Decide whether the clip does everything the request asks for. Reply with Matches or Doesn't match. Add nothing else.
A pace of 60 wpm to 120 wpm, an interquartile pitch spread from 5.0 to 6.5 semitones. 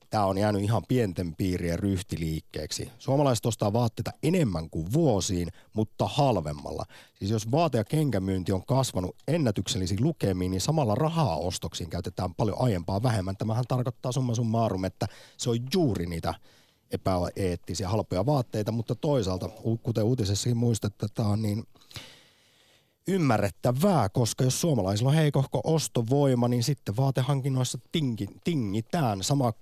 Doesn't match